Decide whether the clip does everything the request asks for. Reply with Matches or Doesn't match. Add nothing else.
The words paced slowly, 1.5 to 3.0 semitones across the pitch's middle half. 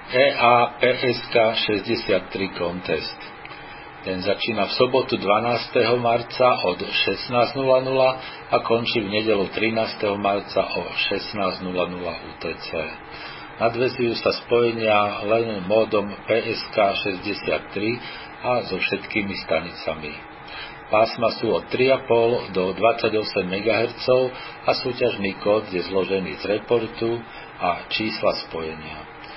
Doesn't match